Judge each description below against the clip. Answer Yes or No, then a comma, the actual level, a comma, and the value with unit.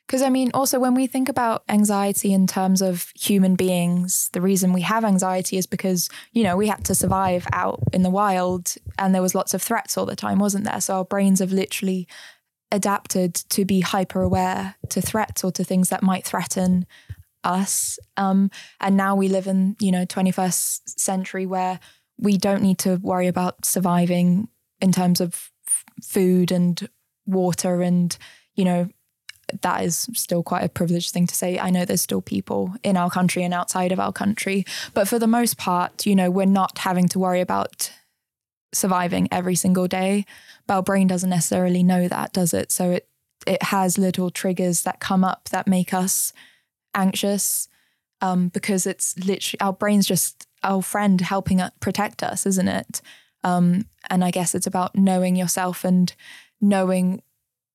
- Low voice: No, medium, 185 Hz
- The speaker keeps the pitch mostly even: Yes, narrow, 1.4 semitones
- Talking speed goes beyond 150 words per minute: Yes, average, 180 wpm